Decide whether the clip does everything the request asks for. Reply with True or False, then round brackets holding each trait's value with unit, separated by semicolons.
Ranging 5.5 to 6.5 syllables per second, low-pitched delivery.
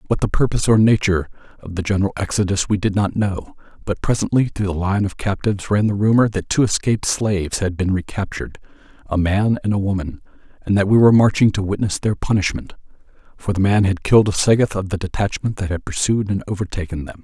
True (6.3 syllables/s; 100 Hz)